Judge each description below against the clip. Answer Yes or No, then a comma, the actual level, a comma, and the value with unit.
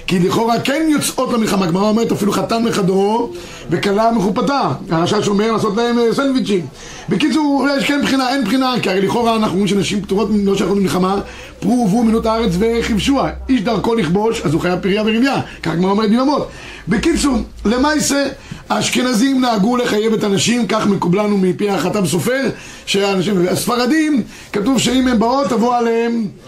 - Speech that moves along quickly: Yes, fast, 155 wpm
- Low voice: No, high, 220 Hz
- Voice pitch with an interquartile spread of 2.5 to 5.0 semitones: Yes, average, 4.0 semitones